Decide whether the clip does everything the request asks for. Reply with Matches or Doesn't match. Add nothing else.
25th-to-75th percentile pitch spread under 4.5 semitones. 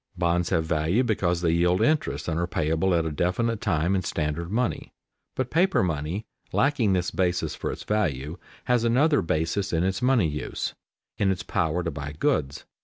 Doesn't match